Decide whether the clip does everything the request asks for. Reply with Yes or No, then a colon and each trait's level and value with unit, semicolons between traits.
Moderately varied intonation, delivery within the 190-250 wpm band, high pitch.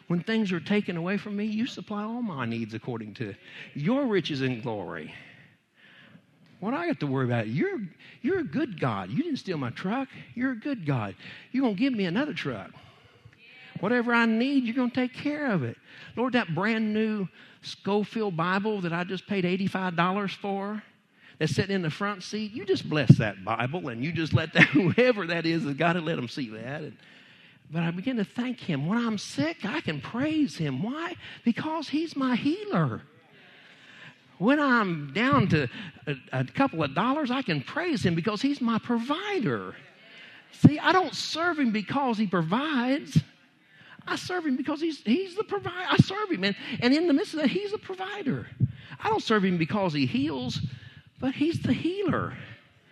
No: wide, 8.6 semitones; average, 195 wpm; high, 210 Hz